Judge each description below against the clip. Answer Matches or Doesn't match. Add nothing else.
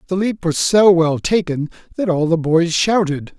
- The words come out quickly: Doesn't match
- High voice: Doesn't match